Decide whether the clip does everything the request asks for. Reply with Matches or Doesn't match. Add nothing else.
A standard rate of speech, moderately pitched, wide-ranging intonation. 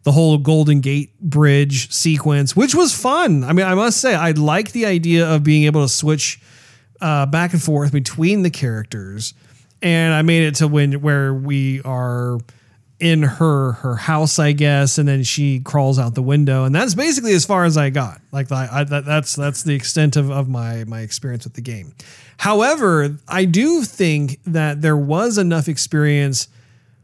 Doesn't match